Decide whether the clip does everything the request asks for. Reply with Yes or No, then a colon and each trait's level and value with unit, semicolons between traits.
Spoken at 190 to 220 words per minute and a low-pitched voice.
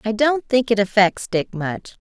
No: fast, 205 wpm; high, 215 Hz